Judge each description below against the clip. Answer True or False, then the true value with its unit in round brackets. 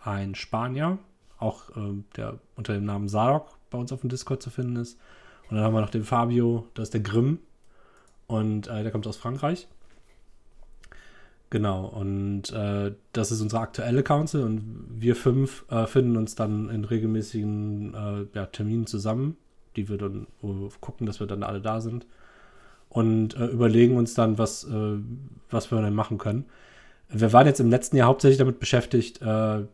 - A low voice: True (110 Hz)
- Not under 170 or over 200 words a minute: True (180 wpm)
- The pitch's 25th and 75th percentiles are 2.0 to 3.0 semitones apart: True (2.6 semitones)